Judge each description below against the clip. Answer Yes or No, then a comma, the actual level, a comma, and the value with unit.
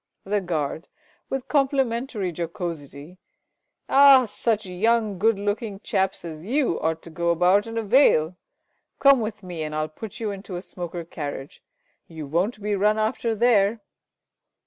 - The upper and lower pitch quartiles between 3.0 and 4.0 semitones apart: No, average, 5.0 semitones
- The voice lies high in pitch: Yes, high, 200 Hz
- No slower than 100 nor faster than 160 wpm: Yes, average, 150 wpm